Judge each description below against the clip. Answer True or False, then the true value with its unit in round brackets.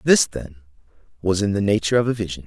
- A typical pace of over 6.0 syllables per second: True (7.0 syllables/s)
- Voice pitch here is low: True (100 Hz)